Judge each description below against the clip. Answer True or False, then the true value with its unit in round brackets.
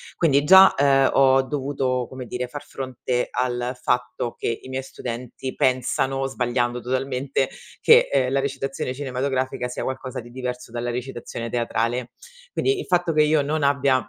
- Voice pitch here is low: True (130 Hz)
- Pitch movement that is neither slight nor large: False (1.8 semitones)